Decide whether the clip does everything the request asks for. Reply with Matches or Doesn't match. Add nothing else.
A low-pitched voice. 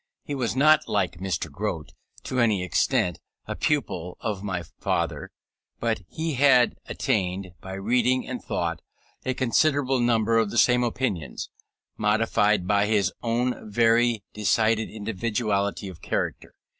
Matches